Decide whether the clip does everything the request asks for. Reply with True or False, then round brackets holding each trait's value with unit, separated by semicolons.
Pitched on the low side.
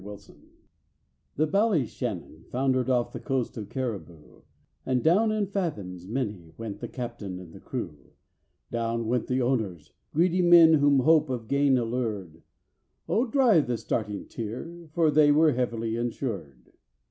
True (125 Hz)